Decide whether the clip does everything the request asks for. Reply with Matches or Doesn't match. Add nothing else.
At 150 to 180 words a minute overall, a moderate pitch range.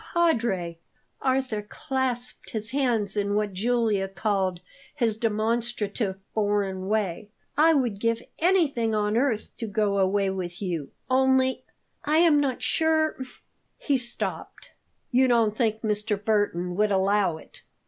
Doesn't match